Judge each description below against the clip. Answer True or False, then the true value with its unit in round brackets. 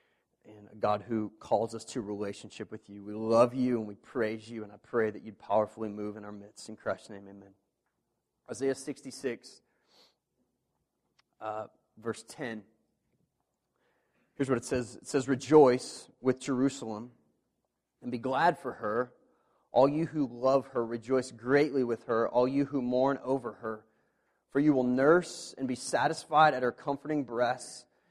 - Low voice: True (120 Hz)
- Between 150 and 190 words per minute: True (160 wpm)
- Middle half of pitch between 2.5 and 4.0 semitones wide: True (3.7 semitones)